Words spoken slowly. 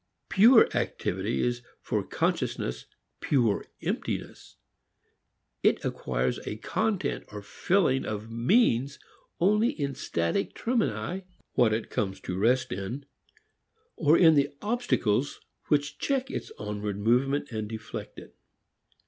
Yes: slow, 115 wpm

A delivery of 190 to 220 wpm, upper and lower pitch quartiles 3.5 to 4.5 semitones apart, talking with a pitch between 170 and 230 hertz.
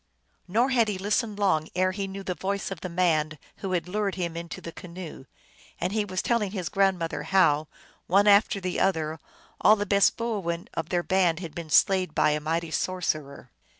No: average, 200 wpm; average, 3.1 semitones; medium, 185 Hz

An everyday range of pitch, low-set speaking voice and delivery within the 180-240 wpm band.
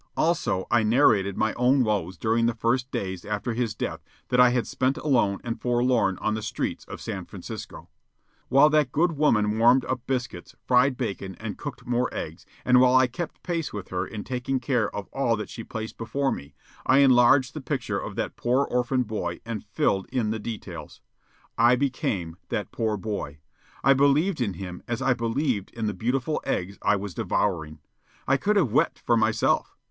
Yes: average, 3.8 semitones; low, 120 Hz; average, 190 wpm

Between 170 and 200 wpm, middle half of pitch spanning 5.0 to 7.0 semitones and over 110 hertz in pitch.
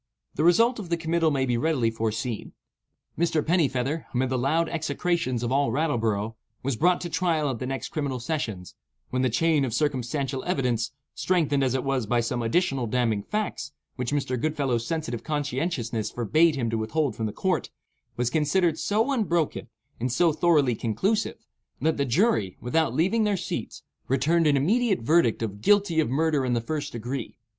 Yes: average, 175 wpm; average, 5.3 semitones; medium, 140 Hz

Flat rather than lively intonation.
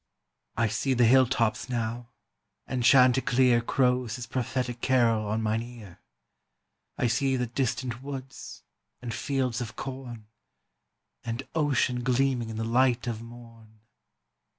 Yes: narrow, 2.1 semitones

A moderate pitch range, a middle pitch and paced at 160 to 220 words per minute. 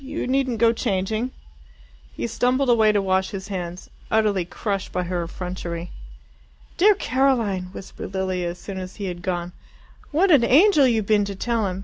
No: average, 4.9 semitones; high, 200 Hz; average, 170 wpm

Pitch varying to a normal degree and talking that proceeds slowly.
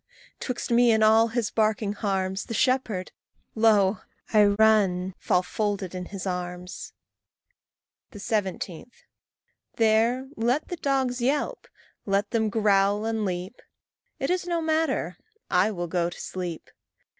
Yes: average, 3.6 semitones; slow, 130 wpm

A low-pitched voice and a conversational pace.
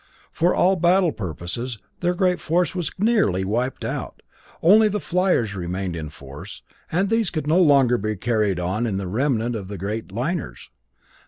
Yes: low, 120 Hz; average, 165 wpm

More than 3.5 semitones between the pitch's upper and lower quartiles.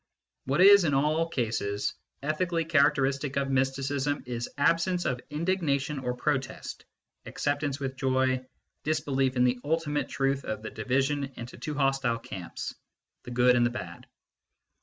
No: average, 2.9 semitones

